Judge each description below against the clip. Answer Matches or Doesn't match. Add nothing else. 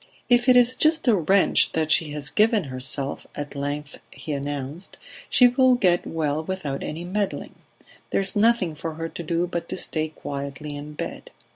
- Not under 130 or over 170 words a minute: Doesn't match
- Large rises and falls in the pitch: Matches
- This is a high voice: Doesn't match